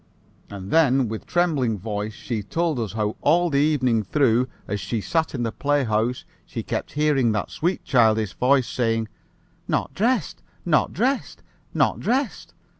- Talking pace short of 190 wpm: Yes, average, 155 wpm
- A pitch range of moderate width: No, wide, 5.8 semitones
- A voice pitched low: Yes, low, 125 Hz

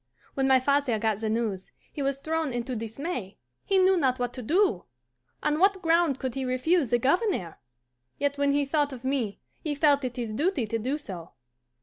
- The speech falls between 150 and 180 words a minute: No, average, 200 wpm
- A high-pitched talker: Yes, very high, 270 Hz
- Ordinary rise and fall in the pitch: Yes, average, 4.5 semitones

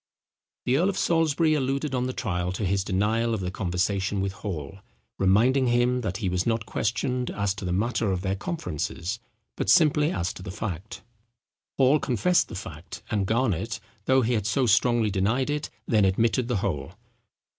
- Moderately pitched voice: No, low, 110 Hz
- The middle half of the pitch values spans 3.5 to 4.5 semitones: No, average, 5.1 semitones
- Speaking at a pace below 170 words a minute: No, average, 180 wpm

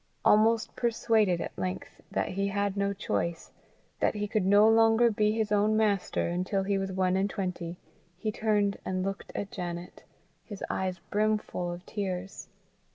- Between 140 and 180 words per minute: Yes, average, 160 wpm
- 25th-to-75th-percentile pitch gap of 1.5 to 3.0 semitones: Yes, narrow, 2.5 semitones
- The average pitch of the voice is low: No, high, 200 Hz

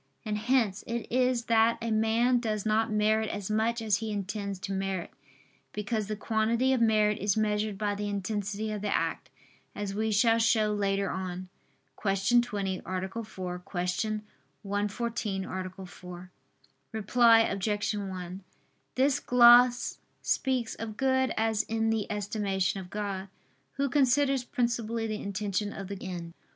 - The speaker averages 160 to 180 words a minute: No, average, 150 wpm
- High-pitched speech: Yes, high, 210 Hz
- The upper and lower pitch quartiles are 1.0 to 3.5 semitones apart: Yes, average, 2.7 semitones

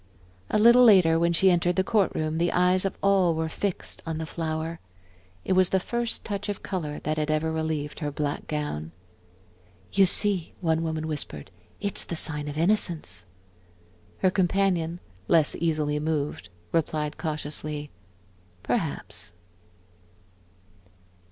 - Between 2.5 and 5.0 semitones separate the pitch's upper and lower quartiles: Yes, average, 3.4 semitones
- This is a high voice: No, medium, 160 Hz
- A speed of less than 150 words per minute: Yes, average, 140 wpm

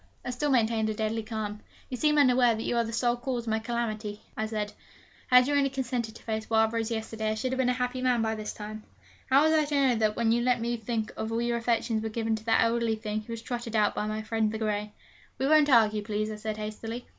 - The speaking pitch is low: No, high, 225 Hz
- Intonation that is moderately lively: No, narrow, 2.2 semitones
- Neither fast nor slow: No, fast, 260 wpm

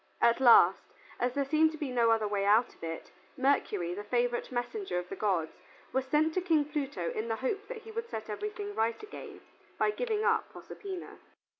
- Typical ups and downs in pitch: No, wide, 9.0 semitones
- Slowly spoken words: No, average, 200 wpm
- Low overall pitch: No, very high, 260 Hz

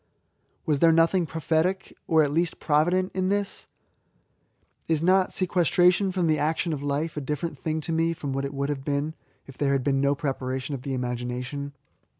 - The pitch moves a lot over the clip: No, average, 3.3 semitones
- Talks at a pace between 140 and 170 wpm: No, average, 185 wpm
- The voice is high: No, medium, 155 Hz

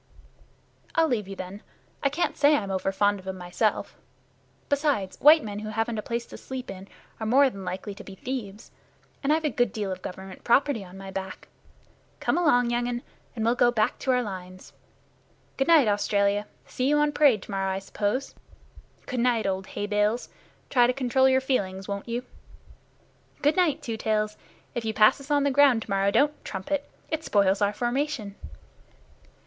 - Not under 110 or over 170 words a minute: No, average, 190 wpm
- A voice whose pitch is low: No, high, 225 Hz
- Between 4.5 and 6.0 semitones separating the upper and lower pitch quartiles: Yes, average, 5.1 semitones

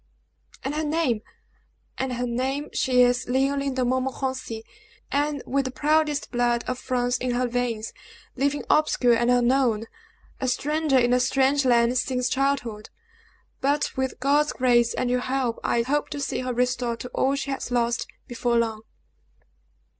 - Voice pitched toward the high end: Yes, very high, 255 Hz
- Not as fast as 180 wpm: Yes, average, 160 wpm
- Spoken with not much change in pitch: Yes, narrow, 2.1 semitones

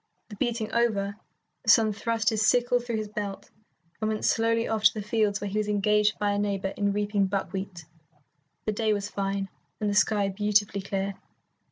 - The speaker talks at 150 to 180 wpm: No, average, 190 wpm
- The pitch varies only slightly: Yes, narrow, 1.6 semitones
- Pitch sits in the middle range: No, high, 210 Hz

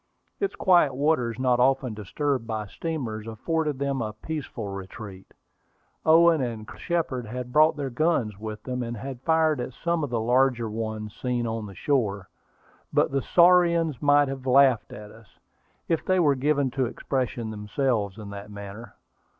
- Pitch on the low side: Yes, low, 125 Hz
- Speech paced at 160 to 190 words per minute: Yes, average, 165 wpm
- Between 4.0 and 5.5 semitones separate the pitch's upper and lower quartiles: Yes, average, 5.0 semitones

